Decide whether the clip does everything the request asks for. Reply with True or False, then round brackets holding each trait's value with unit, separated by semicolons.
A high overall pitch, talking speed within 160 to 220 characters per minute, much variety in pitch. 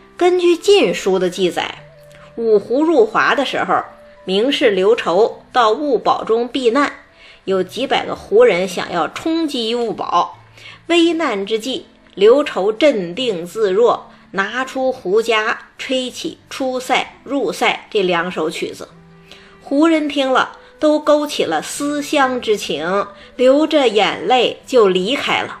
True (260 Hz; 190 characters per minute; 8.1 semitones)